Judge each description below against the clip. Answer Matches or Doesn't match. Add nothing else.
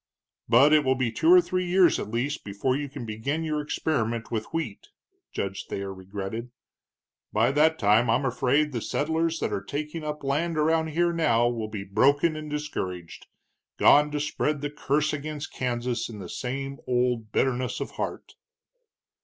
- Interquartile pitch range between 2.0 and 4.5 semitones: Doesn't match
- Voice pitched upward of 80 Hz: Matches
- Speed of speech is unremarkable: Matches